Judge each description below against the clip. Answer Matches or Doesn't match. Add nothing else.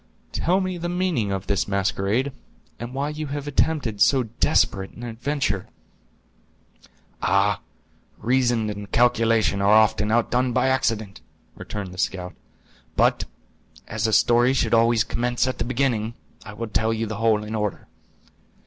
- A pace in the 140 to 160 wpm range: Matches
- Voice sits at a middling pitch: Doesn't match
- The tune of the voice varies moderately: Matches